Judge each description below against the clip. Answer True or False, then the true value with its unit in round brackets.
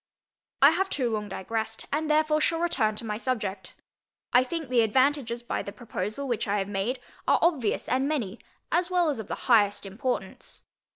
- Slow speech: False (185 wpm)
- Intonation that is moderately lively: False (5.7 semitones)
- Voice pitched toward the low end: False (240 Hz)